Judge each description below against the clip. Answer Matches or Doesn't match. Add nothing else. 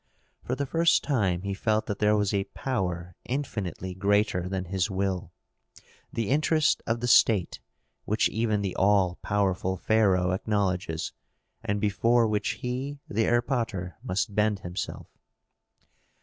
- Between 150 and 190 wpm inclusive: Doesn't match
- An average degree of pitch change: Matches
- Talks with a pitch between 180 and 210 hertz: Doesn't match